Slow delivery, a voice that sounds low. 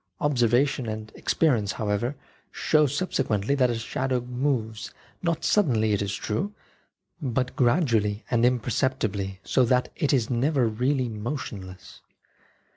Yes: slow, 130 wpm; low, 120 Hz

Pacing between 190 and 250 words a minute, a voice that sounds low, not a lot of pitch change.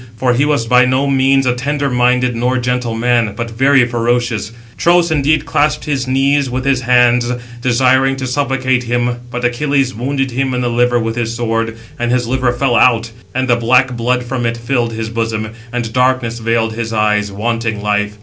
Yes: average, 200 wpm; low, 125 Hz; narrow, 2.1 semitones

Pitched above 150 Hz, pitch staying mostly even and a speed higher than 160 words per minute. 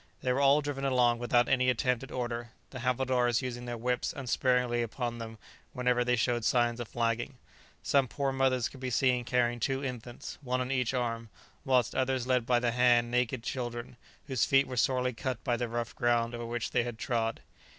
No: low, 125 Hz; narrow, 1.4 semitones; average, 200 wpm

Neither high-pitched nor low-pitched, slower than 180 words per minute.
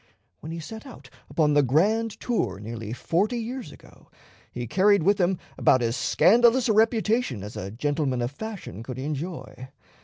Yes: medium, 165 Hz; average, 165 wpm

